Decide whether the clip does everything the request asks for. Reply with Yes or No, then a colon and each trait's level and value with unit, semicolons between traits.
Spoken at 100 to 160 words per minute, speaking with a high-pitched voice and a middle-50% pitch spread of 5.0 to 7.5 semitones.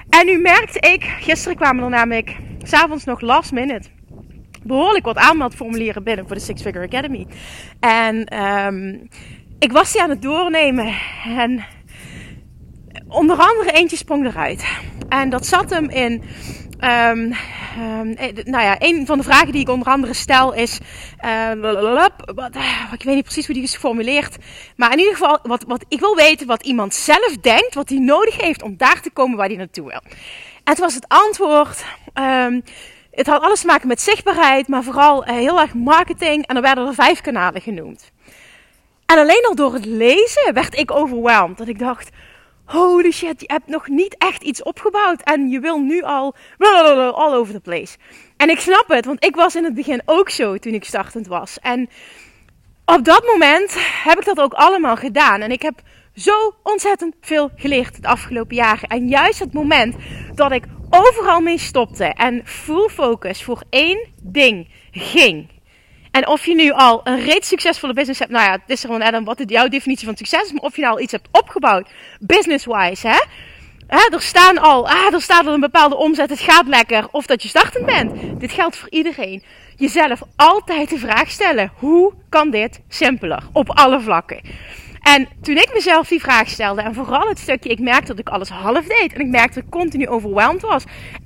No: average, 195 wpm; very high, 280 Hz; wide, 5.5 semitones